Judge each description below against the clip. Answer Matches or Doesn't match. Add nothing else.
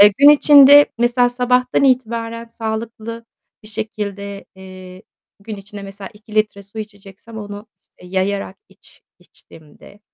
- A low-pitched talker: Doesn't match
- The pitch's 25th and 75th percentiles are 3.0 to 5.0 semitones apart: Doesn't match